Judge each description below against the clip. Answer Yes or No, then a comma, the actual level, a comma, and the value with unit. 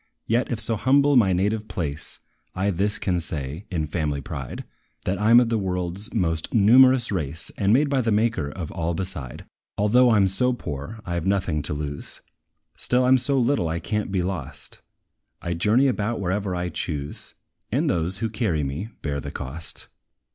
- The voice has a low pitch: Yes, very low, 95 Hz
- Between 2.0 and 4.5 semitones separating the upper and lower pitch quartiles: No, wide, 5.5 semitones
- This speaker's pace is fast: No, average, 190 wpm